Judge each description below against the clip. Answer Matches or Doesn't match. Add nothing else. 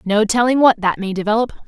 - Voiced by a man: Doesn't match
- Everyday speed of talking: Doesn't match